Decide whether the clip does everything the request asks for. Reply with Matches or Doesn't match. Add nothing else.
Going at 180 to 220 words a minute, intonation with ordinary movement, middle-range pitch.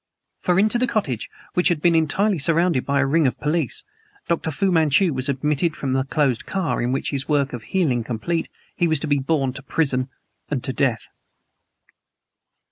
Matches